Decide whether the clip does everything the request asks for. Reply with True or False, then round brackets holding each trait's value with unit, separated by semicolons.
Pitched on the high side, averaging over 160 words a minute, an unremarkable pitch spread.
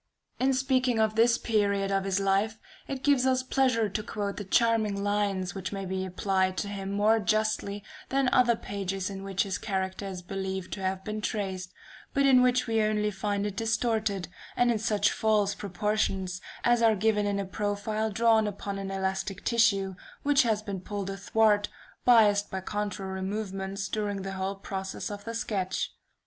False (205 Hz; 180 wpm; 2.3 semitones)